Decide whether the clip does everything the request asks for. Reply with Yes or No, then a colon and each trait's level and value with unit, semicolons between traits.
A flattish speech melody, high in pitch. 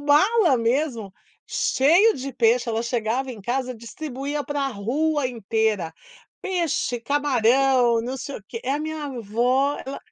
No: average, 3.8 semitones; very high, 260 Hz